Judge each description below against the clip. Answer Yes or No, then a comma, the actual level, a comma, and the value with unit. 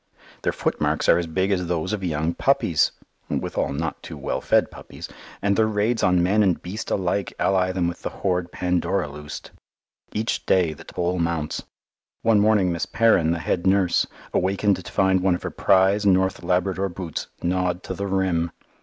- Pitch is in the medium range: No, very low, 90 Hz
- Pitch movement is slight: Yes, narrow, 2.2 semitones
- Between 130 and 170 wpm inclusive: No, average, 180 wpm